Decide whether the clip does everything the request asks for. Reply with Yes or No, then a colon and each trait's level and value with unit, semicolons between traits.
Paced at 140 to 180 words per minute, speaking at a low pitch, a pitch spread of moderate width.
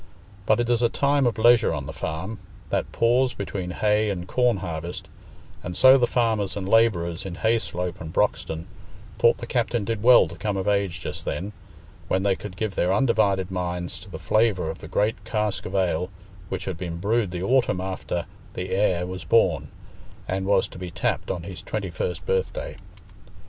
No: average, 190 wpm; very low, 95 Hz; average, 4.1 semitones